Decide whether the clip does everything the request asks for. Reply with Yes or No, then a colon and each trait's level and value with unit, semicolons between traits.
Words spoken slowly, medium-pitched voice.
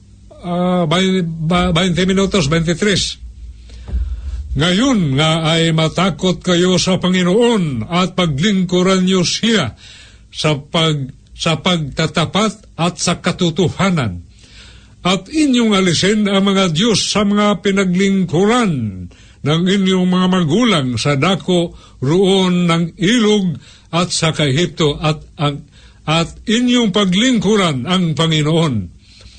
Yes: slow, 100 wpm; medium, 175 Hz